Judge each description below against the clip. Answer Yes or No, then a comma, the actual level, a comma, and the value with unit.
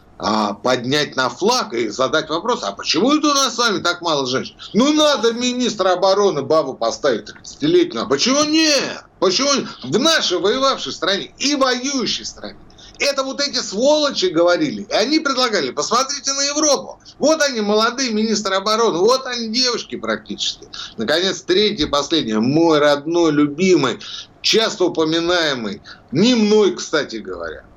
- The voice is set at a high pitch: Yes, high, 215 Hz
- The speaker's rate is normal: Yes, average, 145 wpm